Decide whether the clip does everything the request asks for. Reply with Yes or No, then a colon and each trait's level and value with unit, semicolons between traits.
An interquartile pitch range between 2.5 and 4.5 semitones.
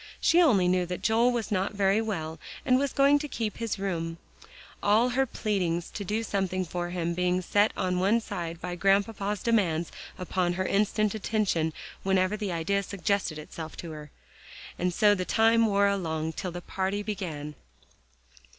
Yes: average, 3.3 semitones